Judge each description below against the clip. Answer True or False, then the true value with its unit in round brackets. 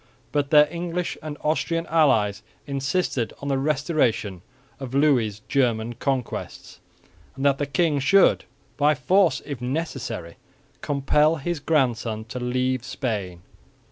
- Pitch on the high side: False (135 Hz)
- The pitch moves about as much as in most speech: True (3.9 semitones)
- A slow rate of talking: True (125 wpm)